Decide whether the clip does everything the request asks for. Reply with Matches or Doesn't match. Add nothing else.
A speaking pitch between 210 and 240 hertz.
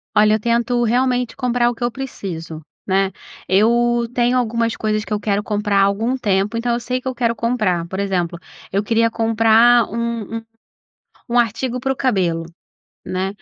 Matches